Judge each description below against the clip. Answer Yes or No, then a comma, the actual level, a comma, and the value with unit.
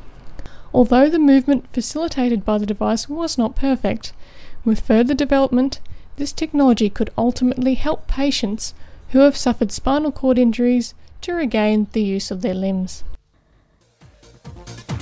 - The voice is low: No, high, 245 Hz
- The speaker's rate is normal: No, slow, 130 wpm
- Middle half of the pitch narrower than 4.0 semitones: No, average, 4.4 semitones